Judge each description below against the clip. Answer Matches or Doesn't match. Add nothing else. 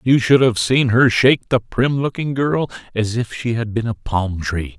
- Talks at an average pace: Doesn't match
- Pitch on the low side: Matches